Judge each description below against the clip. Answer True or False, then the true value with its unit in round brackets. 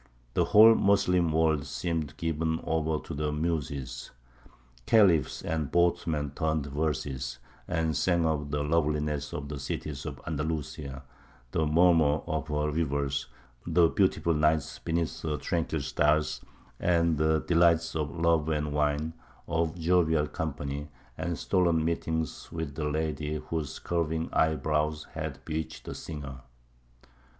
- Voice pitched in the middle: False (80 Hz)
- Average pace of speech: False (130 wpm)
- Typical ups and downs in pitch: False (1.9 semitones)